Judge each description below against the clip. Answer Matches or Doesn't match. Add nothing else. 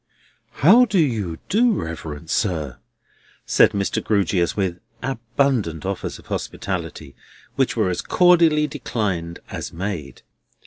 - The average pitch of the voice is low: Matches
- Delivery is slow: Matches